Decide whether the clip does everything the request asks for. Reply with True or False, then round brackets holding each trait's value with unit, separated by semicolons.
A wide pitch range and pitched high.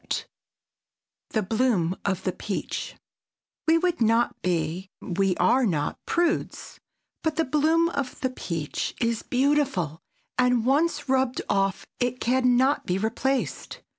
True (6.3 semitones; 245 Hz)